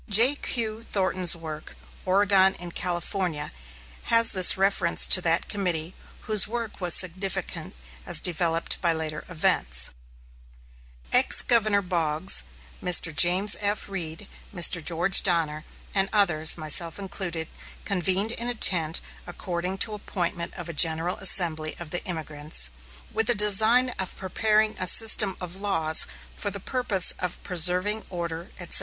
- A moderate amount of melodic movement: Yes, average, 3.4 semitones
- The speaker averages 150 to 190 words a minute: No, slow, 135 wpm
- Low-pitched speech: No, medium, 180 Hz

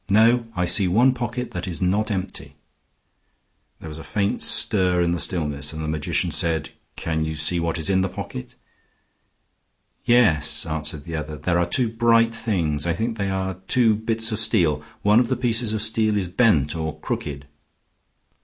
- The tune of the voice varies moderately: No, wide, 5.9 semitones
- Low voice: Yes, very low, 95 Hz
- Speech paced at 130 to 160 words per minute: No, average, 180 wpm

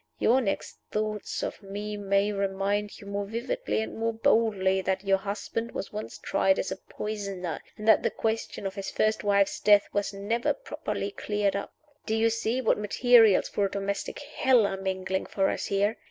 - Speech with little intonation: Yes, narrow, 2.0 semitones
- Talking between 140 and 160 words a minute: No, average, 185 wpm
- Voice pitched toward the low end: No, high, 205 Hz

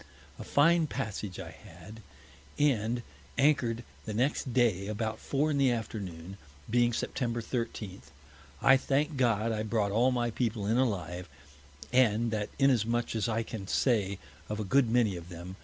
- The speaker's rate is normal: Yes, average, 160 wpm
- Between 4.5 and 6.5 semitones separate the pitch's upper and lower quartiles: No, average, 3.4 semitones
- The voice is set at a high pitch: No, low, 115 Hz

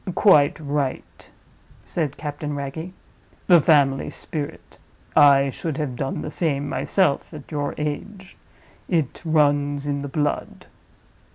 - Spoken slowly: Yes, slow, 120 wpm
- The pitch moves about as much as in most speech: No, narrow, 2.0 semitones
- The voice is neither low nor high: Yes, medium, 145 Hz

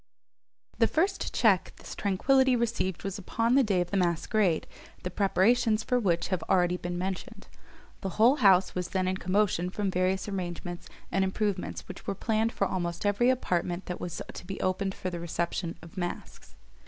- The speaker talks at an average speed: Yes, average, 180 wpm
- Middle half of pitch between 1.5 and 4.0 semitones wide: Yes, average, 3.2 semitones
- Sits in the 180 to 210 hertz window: Yes, high, 190 Hz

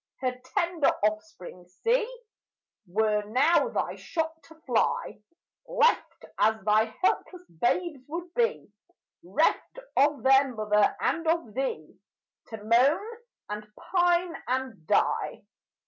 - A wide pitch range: Yes, wide, 8.2 semitones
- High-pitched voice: Yes, very high, 265 Hz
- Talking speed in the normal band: No, slow, 115 wpm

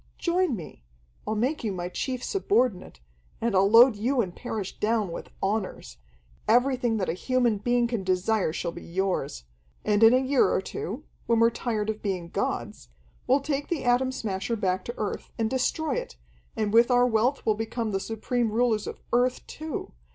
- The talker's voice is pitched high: Yes, high, 225 Hz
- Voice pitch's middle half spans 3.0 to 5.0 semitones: Yes, average, 3.9 semitones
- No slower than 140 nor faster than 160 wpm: No, average, 185 wpm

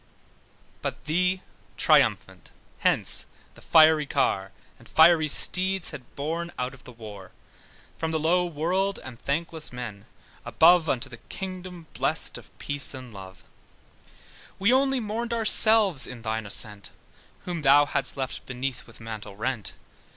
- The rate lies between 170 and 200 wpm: No, average, 140 wpm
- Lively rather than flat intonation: Yes, wide, 6.7 semitones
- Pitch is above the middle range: No, medium, 150 Hz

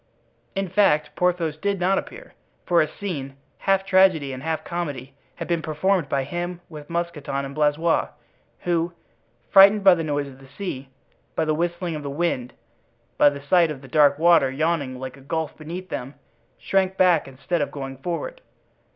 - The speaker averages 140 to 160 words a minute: No, average, 175 wpm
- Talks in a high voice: No, medium, 160 Hz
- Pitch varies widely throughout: No, average, 4.0 semitones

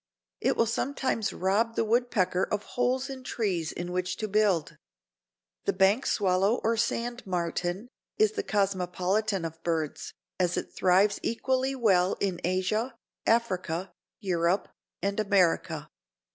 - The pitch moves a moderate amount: Yes, average, 4.3 semitones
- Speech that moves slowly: Yes, slow, 130 wpm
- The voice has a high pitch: Yes, high, 200 Hz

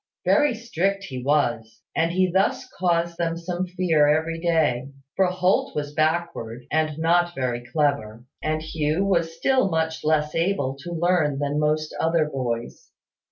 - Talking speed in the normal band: Yes, average, 155 wpm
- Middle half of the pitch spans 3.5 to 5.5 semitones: No, average, 3.0 semitones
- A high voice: No, medium, 160 Hz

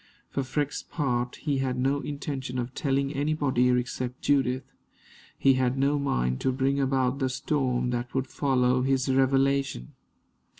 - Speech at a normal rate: Yes, average, 145 wpm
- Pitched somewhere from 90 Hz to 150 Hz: Yes, low, 135 Hz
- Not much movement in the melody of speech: Yes, narrow, 1.6 semitones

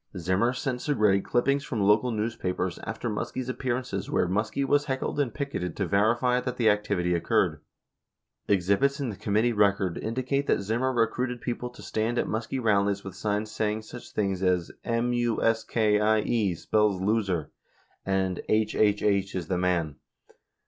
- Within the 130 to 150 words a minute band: No, average, 170 wpm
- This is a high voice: No, low, 110 Hz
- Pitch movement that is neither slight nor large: Yes, average, 3.8 semitones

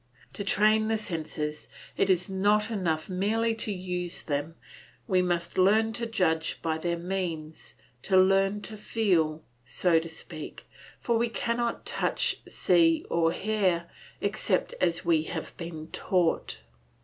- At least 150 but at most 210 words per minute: No, average, 140 wpm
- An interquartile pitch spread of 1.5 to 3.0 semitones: No, average, 4.1 semitones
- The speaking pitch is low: No, medium, 180 Hz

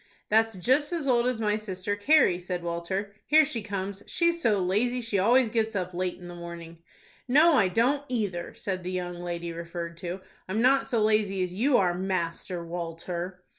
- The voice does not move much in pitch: No, average, 4.8 semitones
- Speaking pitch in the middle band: No, high, 195 Hz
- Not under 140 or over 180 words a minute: No, average, 190 wpm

